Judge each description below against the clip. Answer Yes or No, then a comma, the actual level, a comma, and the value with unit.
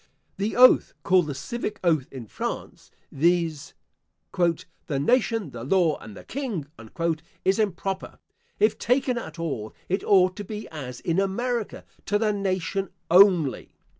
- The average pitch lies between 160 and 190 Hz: Yes, medium, 185 Hz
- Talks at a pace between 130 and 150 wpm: Yes, average, 140 wpm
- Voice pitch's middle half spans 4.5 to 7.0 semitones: Yes, average, 5.1 semitones